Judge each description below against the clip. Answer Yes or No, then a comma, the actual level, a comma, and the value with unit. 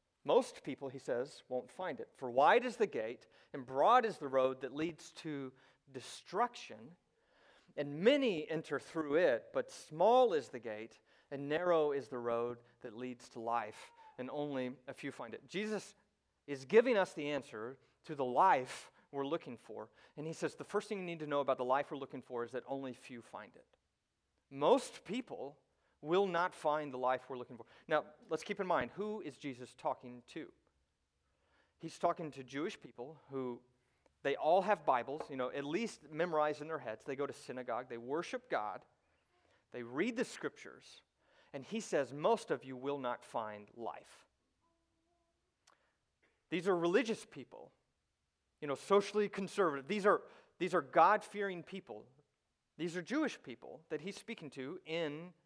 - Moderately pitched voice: Yes, medium, 150 Hz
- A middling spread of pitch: No, wide, 6.7 semitones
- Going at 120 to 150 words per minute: No, average, 175 wpm